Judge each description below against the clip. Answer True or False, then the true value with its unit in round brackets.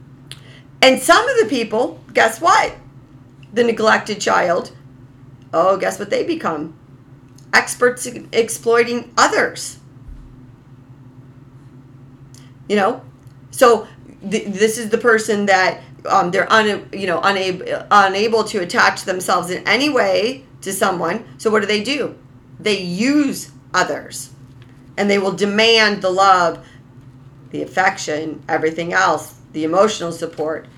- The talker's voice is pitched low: False (165 Hz)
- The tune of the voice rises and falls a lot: True (8.3 semitones)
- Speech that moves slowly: True (125 wpm)